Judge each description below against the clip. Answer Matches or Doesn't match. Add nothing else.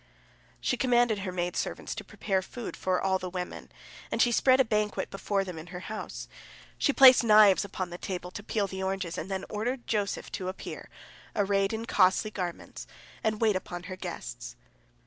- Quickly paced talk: Doesn't match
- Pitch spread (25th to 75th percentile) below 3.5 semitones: Matches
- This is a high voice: Matches